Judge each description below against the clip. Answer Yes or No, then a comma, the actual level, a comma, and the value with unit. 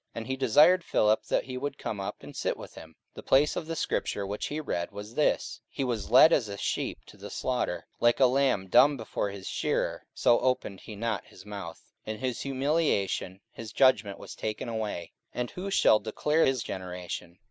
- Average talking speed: No, fast, 215 wpm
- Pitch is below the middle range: Yes, low, 115 Hz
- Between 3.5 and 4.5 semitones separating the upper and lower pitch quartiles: No, average, 5.1 semitones